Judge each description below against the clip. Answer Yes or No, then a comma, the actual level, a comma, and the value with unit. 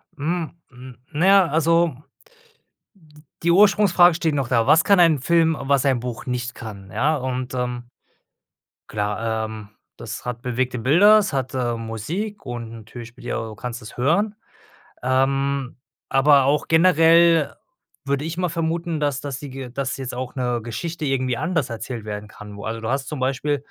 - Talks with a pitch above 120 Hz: Yes, low, 135 Hz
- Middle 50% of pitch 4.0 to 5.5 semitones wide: Yes, average, 5.0 semitones